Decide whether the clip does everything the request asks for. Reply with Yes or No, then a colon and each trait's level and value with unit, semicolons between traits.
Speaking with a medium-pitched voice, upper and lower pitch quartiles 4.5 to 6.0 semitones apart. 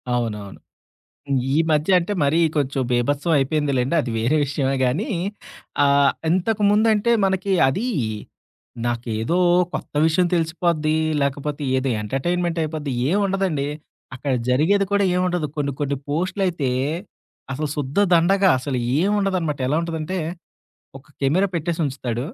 Yes: medium, 155 Hz; average, 4.8 semitones